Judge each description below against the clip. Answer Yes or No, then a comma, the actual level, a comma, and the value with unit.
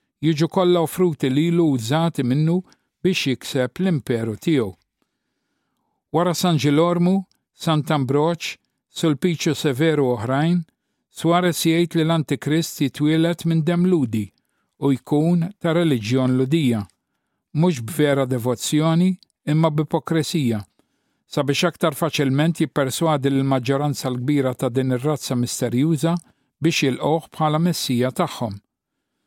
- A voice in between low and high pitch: Yes, medium, 155 Hz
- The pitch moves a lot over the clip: No, average, 3.8 semitones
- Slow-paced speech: Yes, slow, 115 wpm